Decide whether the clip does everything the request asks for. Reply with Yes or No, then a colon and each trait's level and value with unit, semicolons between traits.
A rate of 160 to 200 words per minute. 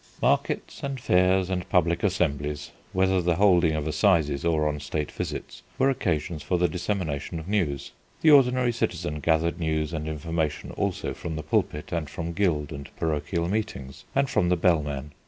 Yes: average, 170 wpm